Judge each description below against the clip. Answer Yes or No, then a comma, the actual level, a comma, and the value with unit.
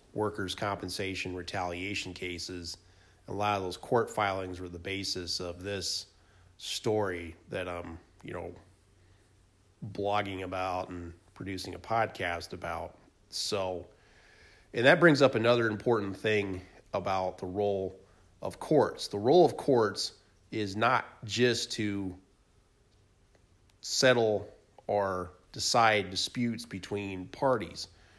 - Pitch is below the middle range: Yes, very low, 95 Hz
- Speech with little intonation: Yes, narrow, 2.2 semitones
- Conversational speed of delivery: No, slow, 115 wpm